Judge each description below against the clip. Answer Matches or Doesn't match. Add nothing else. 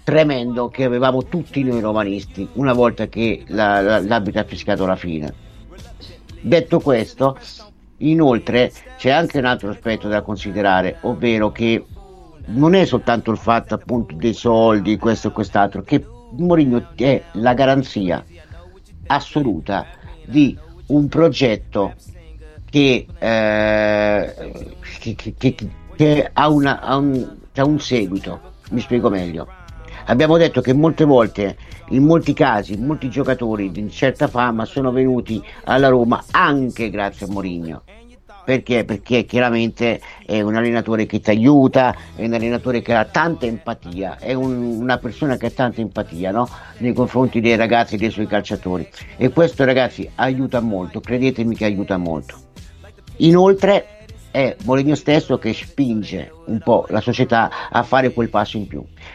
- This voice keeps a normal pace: Matches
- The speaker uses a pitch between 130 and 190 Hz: Doesn't match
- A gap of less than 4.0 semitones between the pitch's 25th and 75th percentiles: Doesn't match